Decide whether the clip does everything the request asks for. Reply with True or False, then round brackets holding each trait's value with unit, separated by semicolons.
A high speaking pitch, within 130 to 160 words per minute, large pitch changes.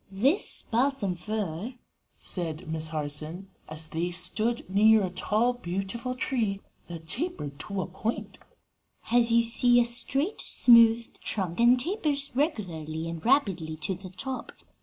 True (205 Hz; 140 wpm; 6.0 semitones)